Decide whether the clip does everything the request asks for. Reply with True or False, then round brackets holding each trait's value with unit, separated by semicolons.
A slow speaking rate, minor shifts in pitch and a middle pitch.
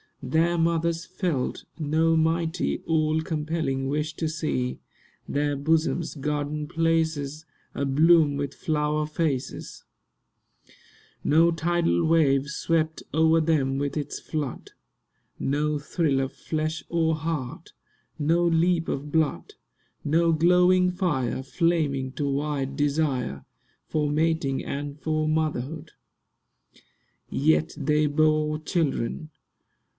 True (105 wpm; 2.2 semitones; 155 Hz)